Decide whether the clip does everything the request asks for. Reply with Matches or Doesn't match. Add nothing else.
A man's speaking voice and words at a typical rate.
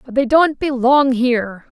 Doesn't match